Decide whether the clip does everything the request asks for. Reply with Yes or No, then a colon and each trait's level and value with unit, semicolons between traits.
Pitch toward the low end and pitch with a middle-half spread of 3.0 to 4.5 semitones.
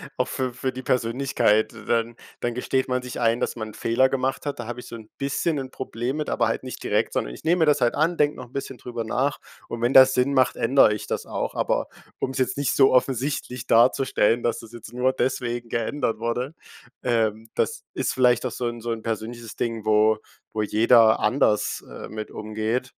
No: low, 120 Hz; narrow, 2.5 semitones